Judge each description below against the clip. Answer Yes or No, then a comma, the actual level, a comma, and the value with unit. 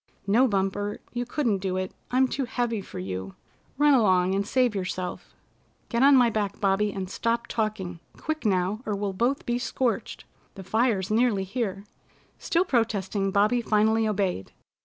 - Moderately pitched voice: No, high, 210 Hz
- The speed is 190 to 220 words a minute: No, average, 160 wpm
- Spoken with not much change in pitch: No, average, 3.8 semitones